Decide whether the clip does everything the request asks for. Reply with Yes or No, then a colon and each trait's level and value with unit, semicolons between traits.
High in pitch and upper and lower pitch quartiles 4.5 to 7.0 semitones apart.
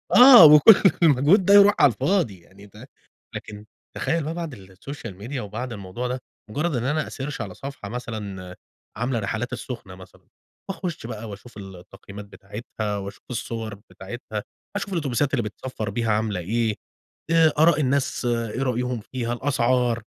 No: low, 120 Hz; average, 5.3 semitones